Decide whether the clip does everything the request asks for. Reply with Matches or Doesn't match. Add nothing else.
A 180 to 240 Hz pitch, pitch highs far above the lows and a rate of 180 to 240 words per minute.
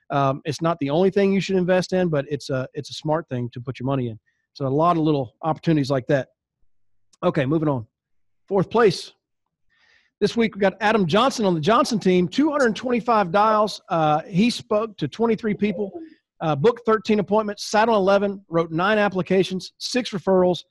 Matches